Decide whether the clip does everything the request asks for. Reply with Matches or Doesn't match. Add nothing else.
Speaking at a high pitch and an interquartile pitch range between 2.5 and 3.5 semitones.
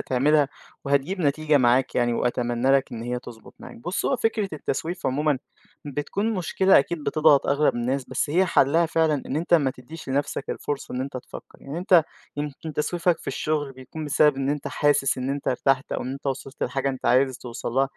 Doesn't match